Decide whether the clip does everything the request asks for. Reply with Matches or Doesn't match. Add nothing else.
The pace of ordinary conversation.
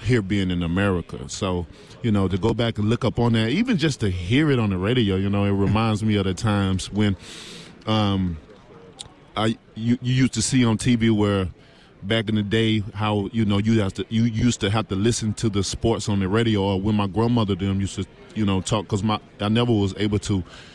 Doesn't match